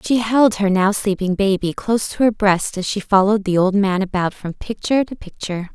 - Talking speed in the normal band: No, fast, 220 wpm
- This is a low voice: No, high, 200 Hz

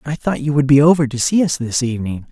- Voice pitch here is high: No, medium, 140 Hz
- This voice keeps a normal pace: No, fast, 310 wpm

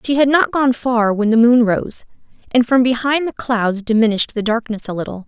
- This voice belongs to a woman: Yes, female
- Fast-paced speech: Yes, fast, 215 wpm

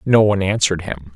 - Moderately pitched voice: No, very low, 95 Hz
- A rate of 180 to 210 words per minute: Yes, fast, 205 wpm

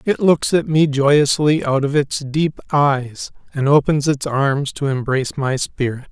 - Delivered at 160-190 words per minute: Yes, average, 175 wpm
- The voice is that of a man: Yes, male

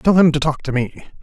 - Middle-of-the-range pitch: Yes, medium, 145 Hz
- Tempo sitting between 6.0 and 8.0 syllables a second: Yes, 6.5 syllables/s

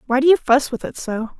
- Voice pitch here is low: No, very high, 260 Hz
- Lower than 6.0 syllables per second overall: No, 6.1 syllables/s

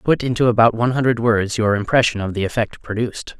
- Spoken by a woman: No, male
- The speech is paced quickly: Yes, fast, 210 wpm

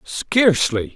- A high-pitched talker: No, medium, 160 Hz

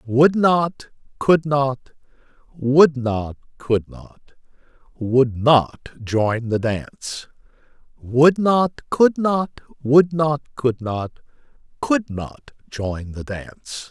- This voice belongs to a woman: No, male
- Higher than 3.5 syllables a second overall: No, 2.8 syllables/s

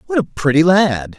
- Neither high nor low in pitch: Yes, medium, 150 Hz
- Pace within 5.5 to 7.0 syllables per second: No, 4.9 syllables/s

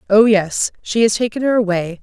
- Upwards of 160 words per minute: Yes, fast, 205 wpm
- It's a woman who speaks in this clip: Yes, female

